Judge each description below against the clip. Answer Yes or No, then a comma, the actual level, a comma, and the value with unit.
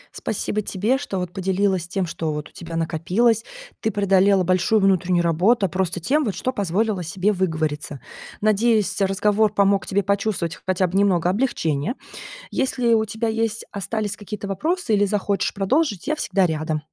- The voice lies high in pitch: Yes, high, 195 Hz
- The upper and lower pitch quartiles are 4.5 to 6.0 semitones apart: No, average, 3.4 semitones